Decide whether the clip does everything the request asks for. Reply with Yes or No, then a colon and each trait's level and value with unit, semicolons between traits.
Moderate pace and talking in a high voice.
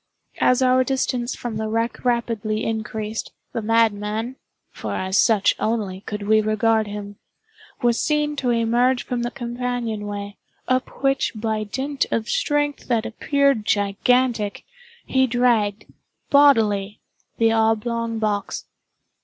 No: slow, 125 wpm; high, 230 Hz